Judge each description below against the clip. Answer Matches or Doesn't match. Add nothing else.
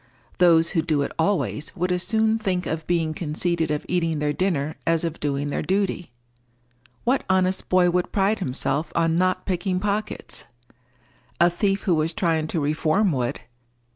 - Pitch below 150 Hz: Doesn't match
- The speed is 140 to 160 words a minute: Doesn't match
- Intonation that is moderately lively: Matches